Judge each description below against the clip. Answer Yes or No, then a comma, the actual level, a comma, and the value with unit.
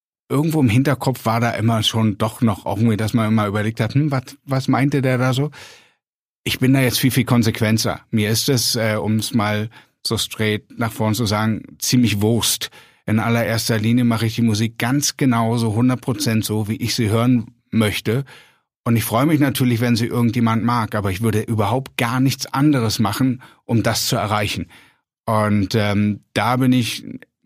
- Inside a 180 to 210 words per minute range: Yes, fast, 190 wpm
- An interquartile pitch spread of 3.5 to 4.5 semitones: No, average, 2.8 semitones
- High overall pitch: No, low, 115 Hz